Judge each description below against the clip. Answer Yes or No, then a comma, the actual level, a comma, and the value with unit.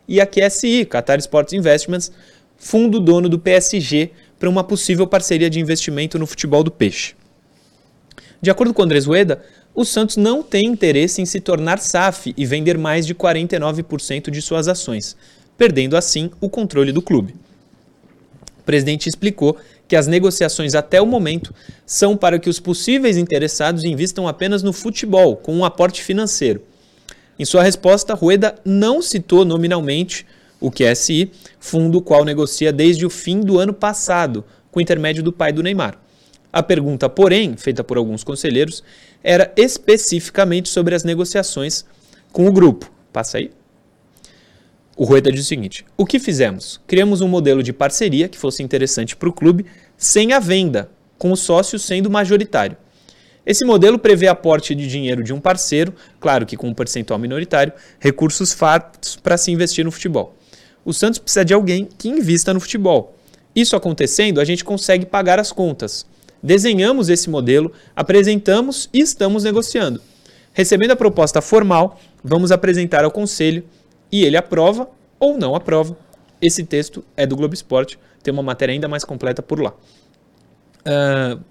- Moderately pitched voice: Yes, medium, 175 Hz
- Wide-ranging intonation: No, average, 4.5 semitones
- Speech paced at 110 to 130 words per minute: No, average, 160 wpm